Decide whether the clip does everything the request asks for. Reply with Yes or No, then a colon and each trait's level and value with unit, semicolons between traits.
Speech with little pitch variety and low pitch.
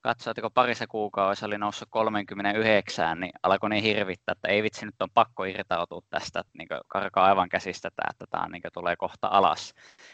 Yes: narrow, 1.7 semitones; low, 105 Hz